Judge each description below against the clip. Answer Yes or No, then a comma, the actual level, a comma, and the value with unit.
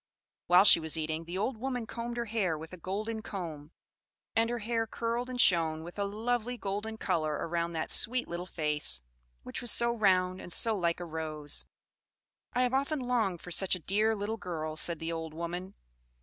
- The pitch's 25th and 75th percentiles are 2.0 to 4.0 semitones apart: No, wide, 5.5 semitones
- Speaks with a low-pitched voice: No, high, 190 Hz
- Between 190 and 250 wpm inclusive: Yes, average, 195 wpm